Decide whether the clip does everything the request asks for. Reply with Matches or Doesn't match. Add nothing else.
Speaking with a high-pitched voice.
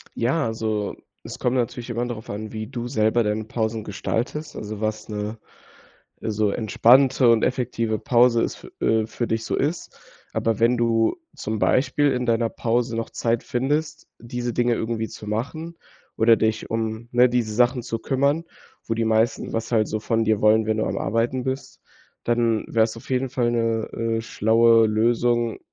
Doesn't match